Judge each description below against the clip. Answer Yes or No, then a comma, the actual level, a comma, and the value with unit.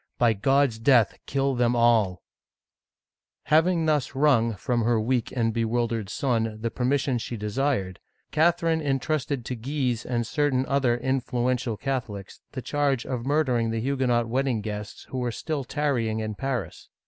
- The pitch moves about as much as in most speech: Yes, average, 3.3 semitones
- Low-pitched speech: Yes, low, 125 Hz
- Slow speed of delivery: No, average, 160 wpm